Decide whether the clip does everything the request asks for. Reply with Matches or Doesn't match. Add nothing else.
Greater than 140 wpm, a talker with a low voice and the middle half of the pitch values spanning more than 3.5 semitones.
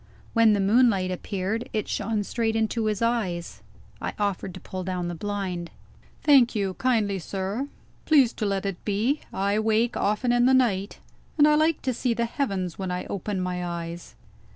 Doesn't match